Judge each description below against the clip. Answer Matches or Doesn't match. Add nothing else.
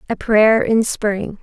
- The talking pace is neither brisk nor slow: Matches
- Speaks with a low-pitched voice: Doesn't match